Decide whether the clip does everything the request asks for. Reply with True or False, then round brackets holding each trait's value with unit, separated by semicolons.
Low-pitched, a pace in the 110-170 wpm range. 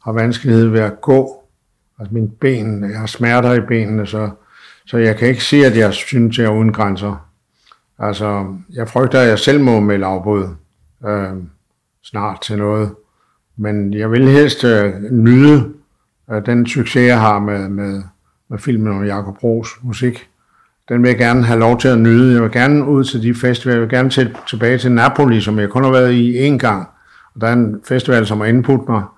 False (115 Hz; 205 wpm)